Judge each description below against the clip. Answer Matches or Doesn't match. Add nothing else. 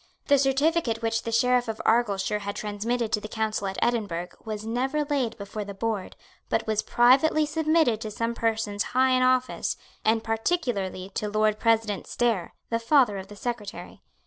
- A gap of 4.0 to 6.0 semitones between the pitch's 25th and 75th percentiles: Doesn't match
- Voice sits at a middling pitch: Doesn't match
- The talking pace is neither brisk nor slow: Matches